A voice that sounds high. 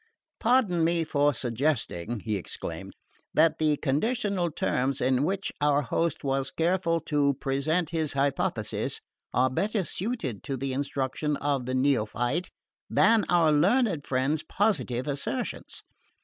No: medium, 145 Hz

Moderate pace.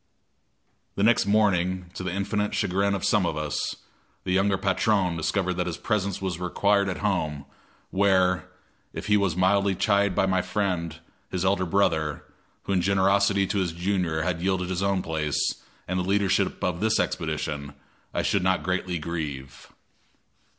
Yes: average, 165 wpm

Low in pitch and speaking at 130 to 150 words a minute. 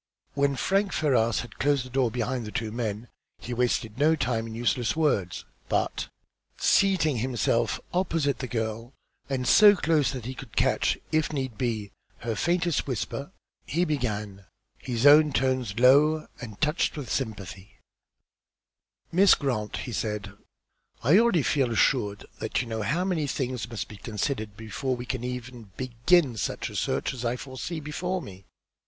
No: low, 125 Hz; average, 160 wpm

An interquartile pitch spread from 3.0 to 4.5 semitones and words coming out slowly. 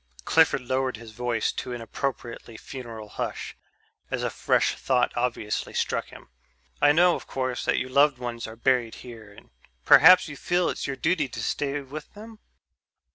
No: average, 3.7 semitones; average, 175 wpm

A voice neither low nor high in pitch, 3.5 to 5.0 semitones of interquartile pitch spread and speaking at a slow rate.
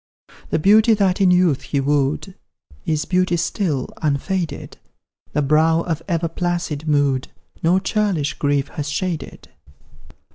Yes: medium, 165 Hz; average, 3.9 semitones; slow, 130 wpm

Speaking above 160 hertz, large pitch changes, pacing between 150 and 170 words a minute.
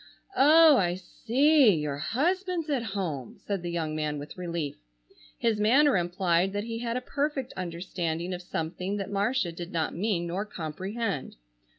Yes: high, 190 Hz; wide, 5.9 semitones; average, 160 wpm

